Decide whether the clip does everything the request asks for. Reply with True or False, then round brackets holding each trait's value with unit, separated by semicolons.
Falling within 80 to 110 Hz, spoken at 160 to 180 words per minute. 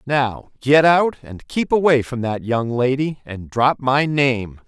False (130 Hz; 165 wpm)